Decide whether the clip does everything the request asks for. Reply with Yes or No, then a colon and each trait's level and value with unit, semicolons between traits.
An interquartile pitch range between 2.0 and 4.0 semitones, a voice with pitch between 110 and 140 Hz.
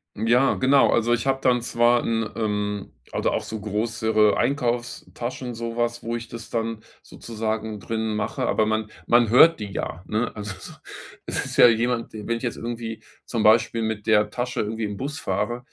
No: narrow, 1.6 semitones; low, 115 Hz